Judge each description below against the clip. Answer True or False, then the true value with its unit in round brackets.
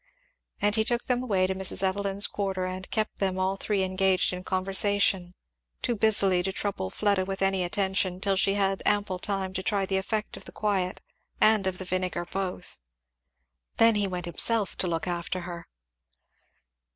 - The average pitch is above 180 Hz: True (190 Hz)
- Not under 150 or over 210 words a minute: True (180 wpm)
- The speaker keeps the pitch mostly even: True (1.6 semitones)